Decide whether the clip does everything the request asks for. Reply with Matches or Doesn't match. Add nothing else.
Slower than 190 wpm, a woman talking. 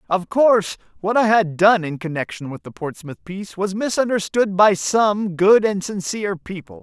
Doesn't match